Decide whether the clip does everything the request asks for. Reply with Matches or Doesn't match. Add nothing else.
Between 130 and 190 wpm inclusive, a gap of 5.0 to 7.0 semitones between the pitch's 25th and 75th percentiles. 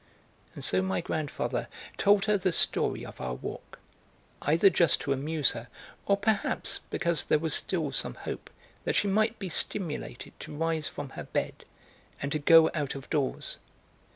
Matches